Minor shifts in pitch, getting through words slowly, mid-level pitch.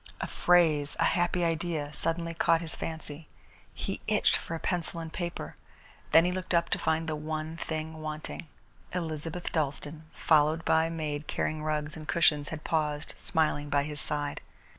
No: narrow, 1.6 semitones; average, 170 wpm; medium, 160 Hz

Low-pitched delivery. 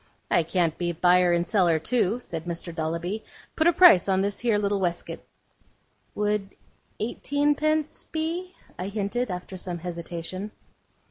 No: high, 195 Hz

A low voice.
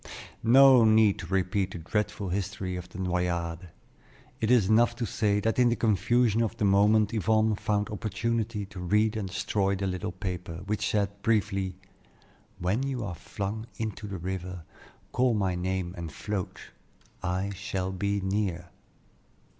Yes: low, 100 Hz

